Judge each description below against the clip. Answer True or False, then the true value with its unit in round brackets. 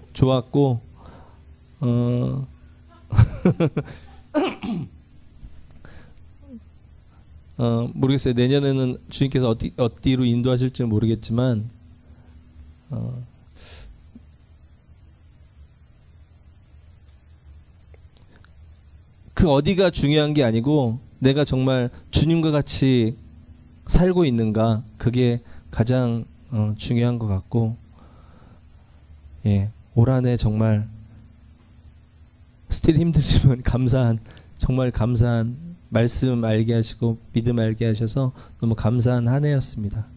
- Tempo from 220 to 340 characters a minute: False (170 characters per minute)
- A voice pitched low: True (110 Hz)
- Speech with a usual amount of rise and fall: False (7.4 semitones)